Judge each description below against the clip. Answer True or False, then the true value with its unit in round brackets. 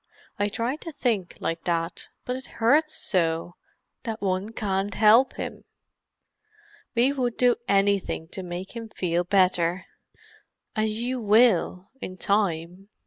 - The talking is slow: True (130 wpm)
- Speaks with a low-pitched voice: False (200 Hz)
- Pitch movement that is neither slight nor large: True (4.5 semitones)